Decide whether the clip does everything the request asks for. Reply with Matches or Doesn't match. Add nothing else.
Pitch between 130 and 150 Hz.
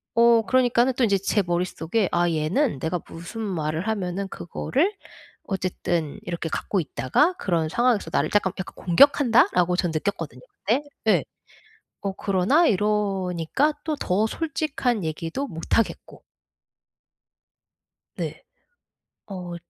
Doesn't match